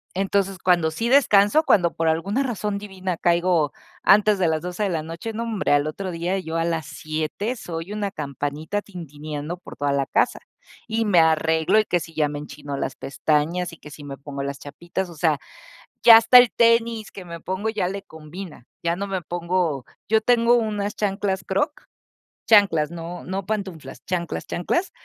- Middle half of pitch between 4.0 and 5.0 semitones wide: Yes, average, 4.4 semitones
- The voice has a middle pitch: Yes, medium, 180 Hz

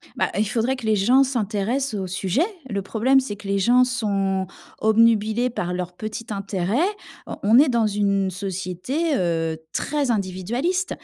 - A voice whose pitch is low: No, high, 215 Hz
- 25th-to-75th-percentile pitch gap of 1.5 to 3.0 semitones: No, average, 4.4 semitones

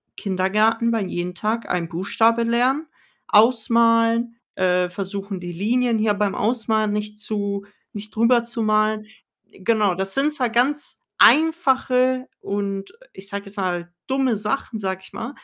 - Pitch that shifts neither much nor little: Yes, average, 3.1 semitones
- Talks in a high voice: Yes, high, 215 Hz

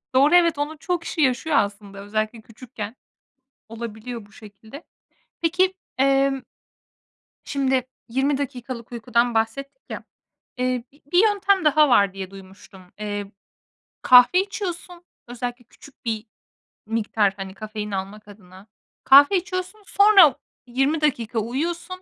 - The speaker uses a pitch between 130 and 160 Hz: No, very high, 250 Hz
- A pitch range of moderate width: No, wide, 6.2 semitones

